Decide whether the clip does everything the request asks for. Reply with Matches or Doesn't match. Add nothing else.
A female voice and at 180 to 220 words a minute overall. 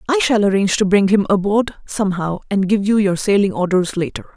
Matches